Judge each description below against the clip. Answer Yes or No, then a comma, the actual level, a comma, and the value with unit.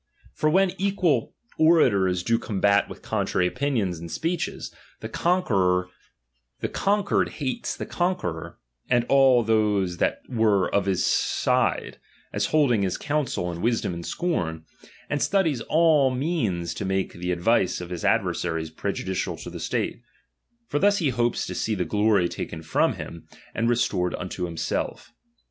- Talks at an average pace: Yes, average, 150 wpm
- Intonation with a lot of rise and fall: Yes, wide, 8.2 semitones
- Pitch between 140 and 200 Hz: No, low, 110 Hz